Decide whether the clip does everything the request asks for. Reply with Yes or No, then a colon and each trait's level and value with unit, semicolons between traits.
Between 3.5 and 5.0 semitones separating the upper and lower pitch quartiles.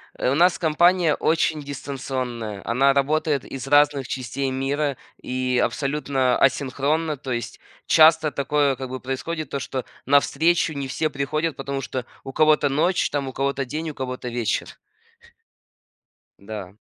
No: average, 2.8 semitones